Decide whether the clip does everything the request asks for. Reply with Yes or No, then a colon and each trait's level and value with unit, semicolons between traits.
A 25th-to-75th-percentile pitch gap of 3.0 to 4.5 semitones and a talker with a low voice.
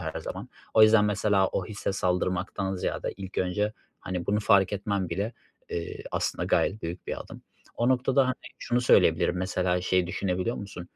No: narrow, 2.6 semitones; very low, 95 Hz